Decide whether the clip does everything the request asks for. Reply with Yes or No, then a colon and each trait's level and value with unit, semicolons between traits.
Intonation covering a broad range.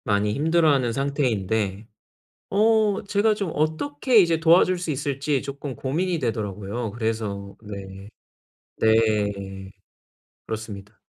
Yes: wide, 7.7 semitones